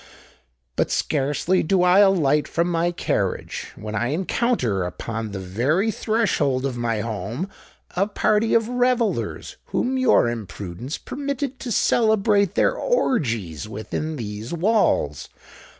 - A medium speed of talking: No, slow, 125 wpm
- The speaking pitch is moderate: Yes, medium, 160 Hz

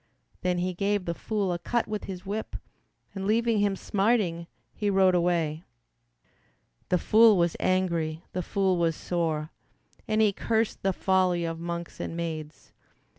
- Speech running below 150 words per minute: No, average, 155 wpm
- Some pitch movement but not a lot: Yes, average, 3.2 semitones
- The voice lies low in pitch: No, medium, 185 Hz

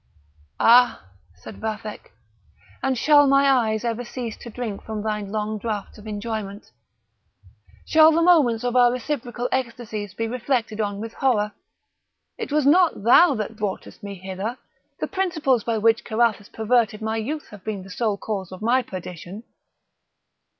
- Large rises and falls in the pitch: No, average, 3.1 semitones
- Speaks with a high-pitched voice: Yes, high, 225 Hz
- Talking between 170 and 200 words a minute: No, average, 155 wpm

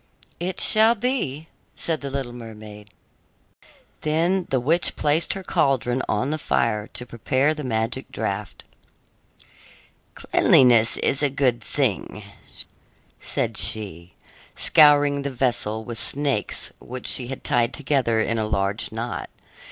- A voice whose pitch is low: Yes, low, 130 Hz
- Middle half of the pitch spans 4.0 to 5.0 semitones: Yes, average, 4.7 semitones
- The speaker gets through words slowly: Yes, slow, 130 wpm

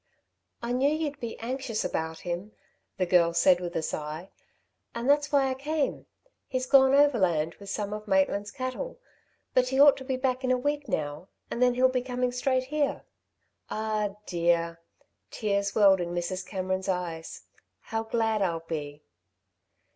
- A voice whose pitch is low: No, high, 215 Hz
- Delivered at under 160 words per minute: No, average, 165 wpm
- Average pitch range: No, wide, 6.5 semitones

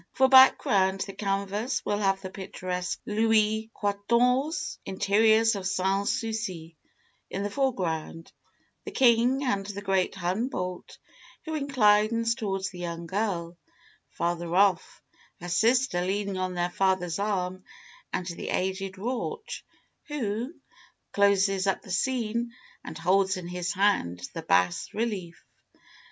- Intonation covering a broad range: No, average, 3.5 semitones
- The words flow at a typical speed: No, slow, 125 wpm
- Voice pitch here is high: Yes, high, 195 Hz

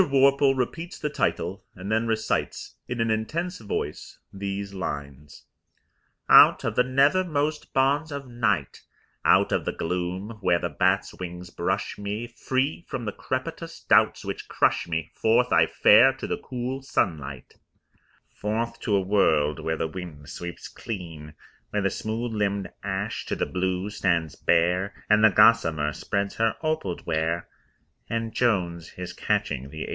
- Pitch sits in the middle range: No, low, 100 Hz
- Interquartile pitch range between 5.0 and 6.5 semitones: Yes, wide, 5.5 semitones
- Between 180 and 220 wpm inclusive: No, average, 155 wpm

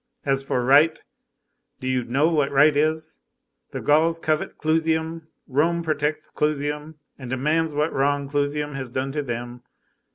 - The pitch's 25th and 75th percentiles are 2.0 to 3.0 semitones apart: Yes, narrow, 2.5 semitones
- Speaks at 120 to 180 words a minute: Yes, average, 150 wpm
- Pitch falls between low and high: Yes, medium, 150 Hz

